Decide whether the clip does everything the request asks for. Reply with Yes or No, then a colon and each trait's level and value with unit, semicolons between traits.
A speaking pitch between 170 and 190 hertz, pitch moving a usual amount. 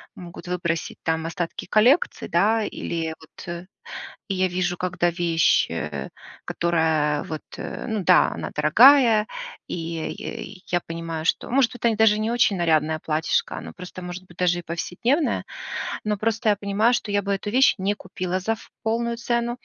Yes: medium, 185 Hz; average, 4.6 semitones